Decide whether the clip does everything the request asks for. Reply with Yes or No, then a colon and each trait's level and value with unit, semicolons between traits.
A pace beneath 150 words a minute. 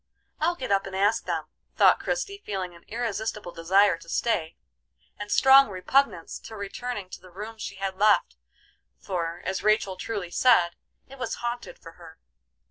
No: average, 165 wpm